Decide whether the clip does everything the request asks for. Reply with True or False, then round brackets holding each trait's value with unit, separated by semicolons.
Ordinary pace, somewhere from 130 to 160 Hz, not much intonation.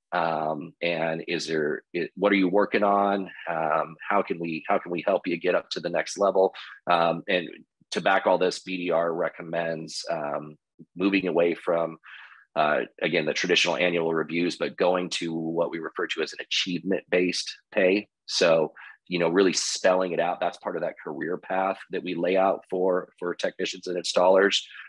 False (185 wpm; 85 Hz; 2.2 semitones)